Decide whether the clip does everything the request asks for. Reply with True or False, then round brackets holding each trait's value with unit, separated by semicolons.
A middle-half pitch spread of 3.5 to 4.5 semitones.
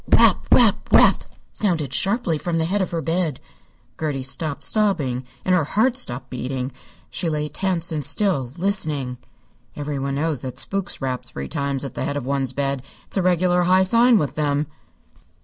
False (5.0 semitones)